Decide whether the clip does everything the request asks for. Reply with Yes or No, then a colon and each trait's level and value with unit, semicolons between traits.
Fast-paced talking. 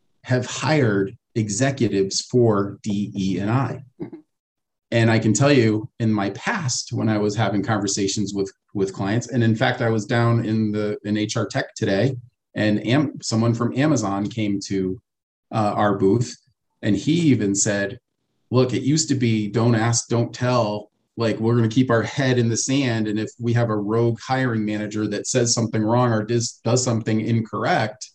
No: average, 185 wpm